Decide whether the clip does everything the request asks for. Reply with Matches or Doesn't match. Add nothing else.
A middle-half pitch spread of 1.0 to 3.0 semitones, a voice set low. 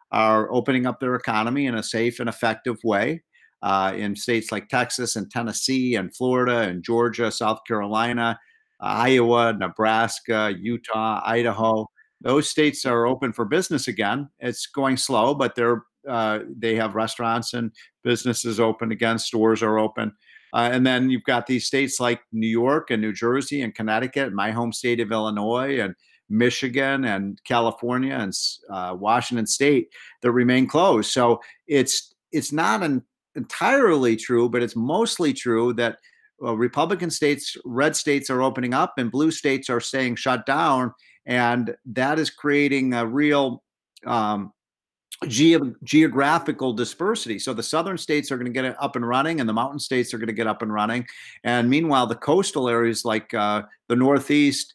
Matches